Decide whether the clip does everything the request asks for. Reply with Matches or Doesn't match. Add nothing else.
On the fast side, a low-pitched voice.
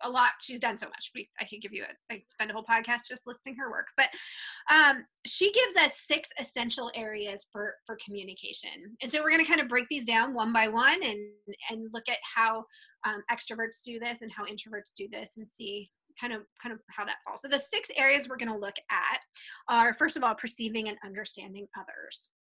Doesn't match